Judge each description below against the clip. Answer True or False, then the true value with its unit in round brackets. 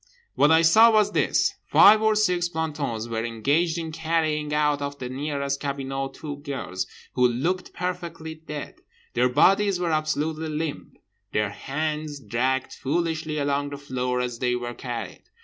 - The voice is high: False (150 Hz)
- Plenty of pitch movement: False (3.5 semitones)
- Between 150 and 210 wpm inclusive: True (155 wpm)